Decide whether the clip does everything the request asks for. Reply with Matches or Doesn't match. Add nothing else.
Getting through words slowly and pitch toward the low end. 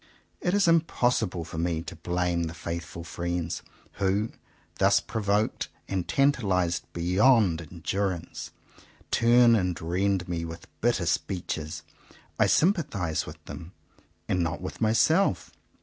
Matches